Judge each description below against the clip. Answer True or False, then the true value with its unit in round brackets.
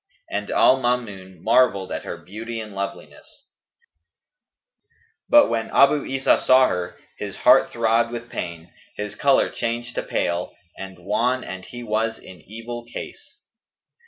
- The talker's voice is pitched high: False (115 Hz)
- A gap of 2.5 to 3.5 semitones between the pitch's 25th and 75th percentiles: False (4.0 semitones)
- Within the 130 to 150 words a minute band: True (140 wpm)